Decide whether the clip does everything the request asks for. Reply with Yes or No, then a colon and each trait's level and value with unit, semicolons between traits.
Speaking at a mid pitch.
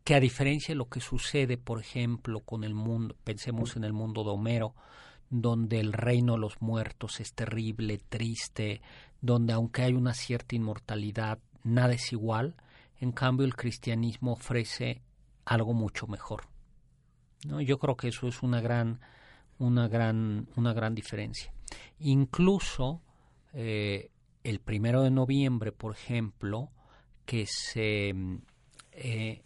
No: low, 115 Hz